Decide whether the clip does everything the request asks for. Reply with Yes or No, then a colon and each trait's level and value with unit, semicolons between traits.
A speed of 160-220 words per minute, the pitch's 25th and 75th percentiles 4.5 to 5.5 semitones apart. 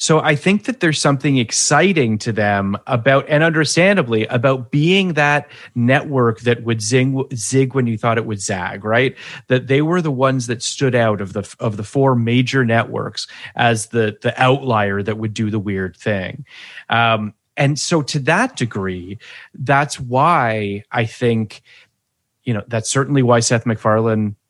No: average, 170 wpm; average, 4.0 semitones